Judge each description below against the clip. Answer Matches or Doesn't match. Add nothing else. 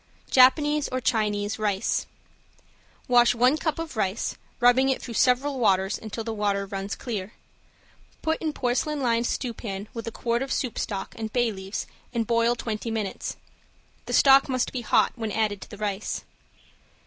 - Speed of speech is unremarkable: Matches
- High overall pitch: Matches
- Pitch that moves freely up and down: Doesn't match